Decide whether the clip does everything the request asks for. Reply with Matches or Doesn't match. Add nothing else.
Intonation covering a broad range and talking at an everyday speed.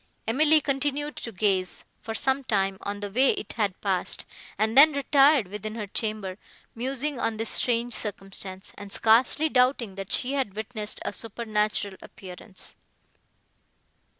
Doesn't match